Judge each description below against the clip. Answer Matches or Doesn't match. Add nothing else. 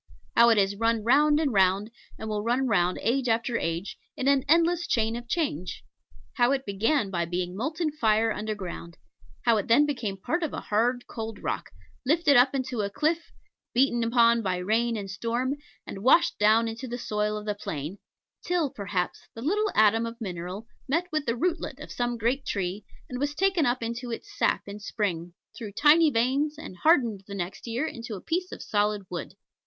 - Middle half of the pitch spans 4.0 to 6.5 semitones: Matches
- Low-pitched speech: Doesn't match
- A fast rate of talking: Doesn't match